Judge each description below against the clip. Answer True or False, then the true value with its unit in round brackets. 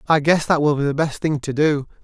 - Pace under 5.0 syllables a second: False (5.8 syllables/s)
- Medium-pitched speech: True (150 Hz)